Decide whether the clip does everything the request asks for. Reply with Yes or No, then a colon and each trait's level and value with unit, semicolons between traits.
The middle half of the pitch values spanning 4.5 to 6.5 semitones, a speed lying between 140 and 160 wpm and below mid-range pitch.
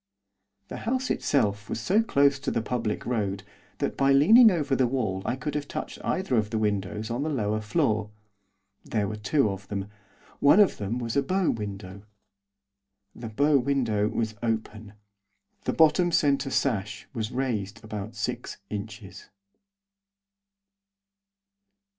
Yes: average, 5.0 semitones; average, 145 wpm; low, 115 Hz